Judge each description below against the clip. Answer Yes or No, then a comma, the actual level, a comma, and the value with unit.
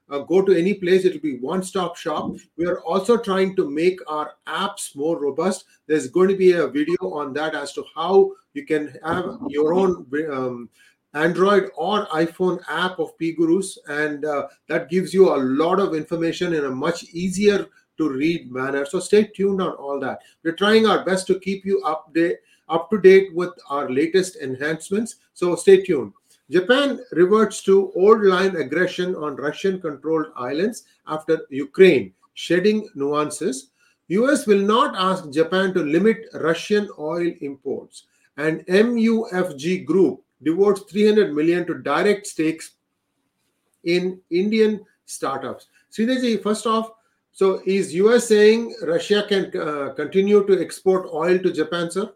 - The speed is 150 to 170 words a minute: Yes, average, 160 wpm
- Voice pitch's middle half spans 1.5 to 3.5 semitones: No, average, 4.5 semitones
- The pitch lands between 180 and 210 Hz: Yes, medium, 185 Hz